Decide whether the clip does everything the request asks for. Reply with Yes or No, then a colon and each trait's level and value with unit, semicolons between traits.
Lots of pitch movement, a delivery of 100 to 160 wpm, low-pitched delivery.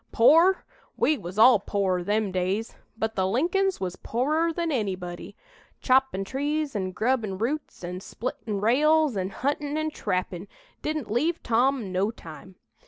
No: wide, 7.5 semitones; average, 145 wpm; high, 230 Hz